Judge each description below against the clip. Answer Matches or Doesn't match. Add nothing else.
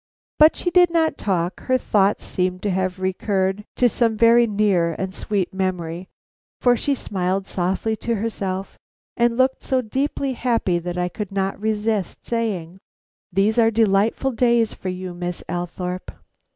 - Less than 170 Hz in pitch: Doesn't match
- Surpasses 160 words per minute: Doesn't match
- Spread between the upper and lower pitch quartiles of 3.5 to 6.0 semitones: Matches